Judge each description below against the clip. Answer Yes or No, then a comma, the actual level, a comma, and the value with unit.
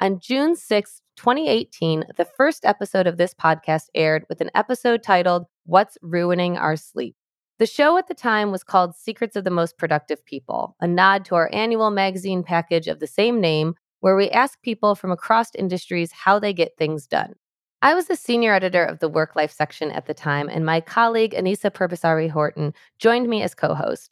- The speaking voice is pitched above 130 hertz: Yes, medium, 185 Hz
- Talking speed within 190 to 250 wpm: Yes, average, 195 wpm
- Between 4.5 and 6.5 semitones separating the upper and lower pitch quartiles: Yes, average, 5.2 semitones